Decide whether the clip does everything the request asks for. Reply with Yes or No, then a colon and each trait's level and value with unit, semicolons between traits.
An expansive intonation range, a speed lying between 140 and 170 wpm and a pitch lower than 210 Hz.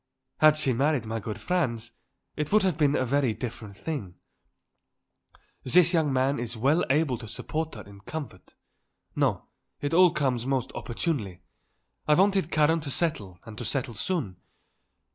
Yes: wide, 5.7 semitones; average, 160 wpm; medium, 140 Hz